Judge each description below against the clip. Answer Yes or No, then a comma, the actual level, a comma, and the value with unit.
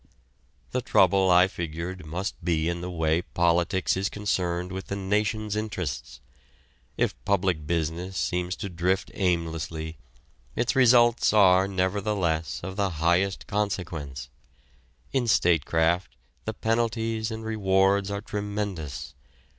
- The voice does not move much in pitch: No, average, 3.4 semitones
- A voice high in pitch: No, very low, 95 Hz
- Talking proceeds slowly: Yes, slow, 120 wpm